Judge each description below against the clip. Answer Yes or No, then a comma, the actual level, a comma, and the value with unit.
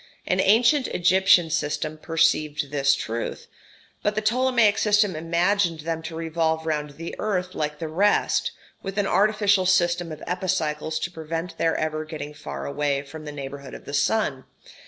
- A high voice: No, medium, 165 Hz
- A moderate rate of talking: Yes, average, 160 wpm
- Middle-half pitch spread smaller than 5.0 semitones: Yes, average, 3.9 semitones